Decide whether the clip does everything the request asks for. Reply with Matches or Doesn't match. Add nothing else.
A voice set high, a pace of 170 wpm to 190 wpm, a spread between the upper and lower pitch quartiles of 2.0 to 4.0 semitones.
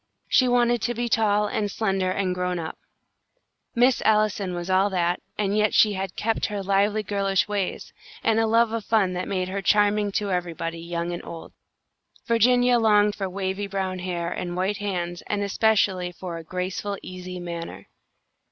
Matches